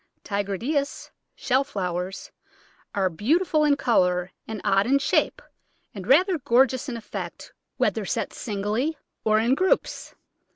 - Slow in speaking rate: Yes, slow, 125 wpm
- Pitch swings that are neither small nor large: No, wide, 6.1 semitones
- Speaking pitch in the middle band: No, high, 235 Hz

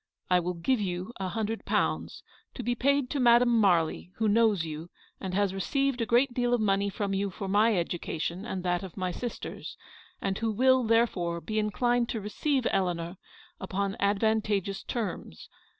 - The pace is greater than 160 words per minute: Yes, average, 175 wpm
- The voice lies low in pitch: No, high, 205 Hz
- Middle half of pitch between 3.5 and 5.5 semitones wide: Yes, average, 4.3 semitones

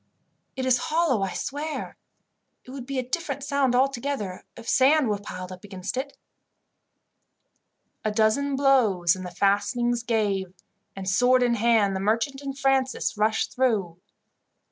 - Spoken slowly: No, average, 145 wpm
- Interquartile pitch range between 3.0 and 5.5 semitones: Yes, average, 5.1 semitones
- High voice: Yes, high, 240 Hz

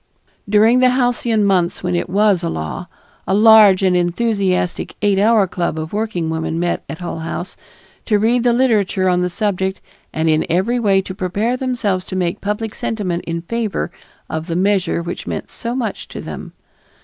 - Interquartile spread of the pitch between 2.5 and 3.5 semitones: No, average, 3.9 semitones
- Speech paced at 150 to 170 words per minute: No, average, 185 wpm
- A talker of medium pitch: No, high, 195 Hz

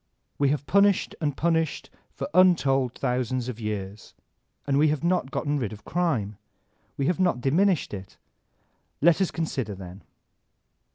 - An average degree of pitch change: No, wide, 6.3 semitones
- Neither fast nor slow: Yes, average, 150 wpm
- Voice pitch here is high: No, medium, 140 Hz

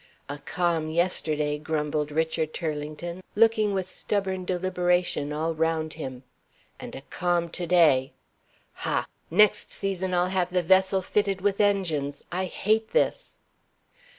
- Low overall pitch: No, medium, 175 Hz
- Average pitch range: Yes, average, 3.2 semitones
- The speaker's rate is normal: No, slow, 130 wpm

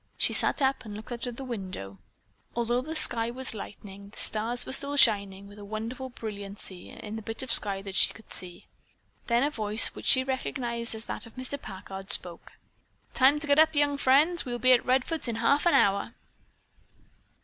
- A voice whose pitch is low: No, high, 235 Hz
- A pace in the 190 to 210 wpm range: Yes, average, 200 wpm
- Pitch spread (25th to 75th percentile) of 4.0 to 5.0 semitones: Yes, average, 4.3 semitones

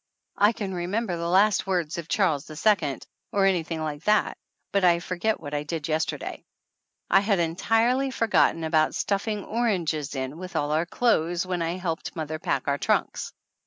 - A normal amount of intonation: Yes, average, 4.3 semitones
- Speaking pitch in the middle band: Yes, medium, 175 Hz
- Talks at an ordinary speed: Yes, average, 185 wpm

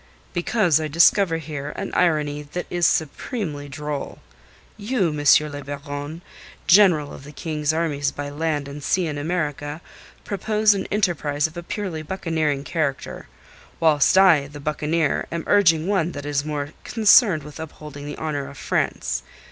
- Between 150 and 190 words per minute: Yes, average, 155 wpm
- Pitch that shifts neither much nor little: Yes, average, 3.2 semitones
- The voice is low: No, medium, 155 Hz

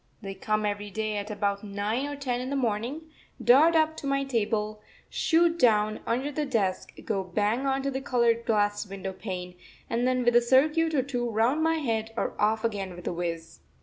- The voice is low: No, high, 230 Hz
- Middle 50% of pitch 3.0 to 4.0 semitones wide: No, average, 4.6 semitones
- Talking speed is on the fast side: Yes, fast, 210 wpm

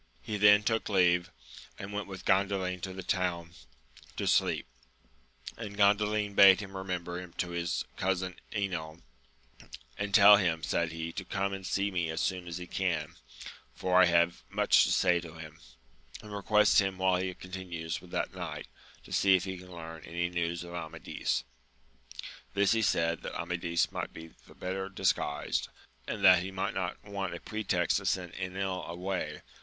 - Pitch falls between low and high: No, very low, 90 Hz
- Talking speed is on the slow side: No, average, 175 wpm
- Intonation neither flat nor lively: No, narrow, 2.2 semitones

